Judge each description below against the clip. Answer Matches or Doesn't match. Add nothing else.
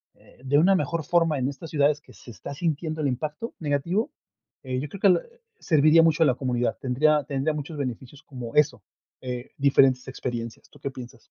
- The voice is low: Doesn't match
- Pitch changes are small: Doesn't match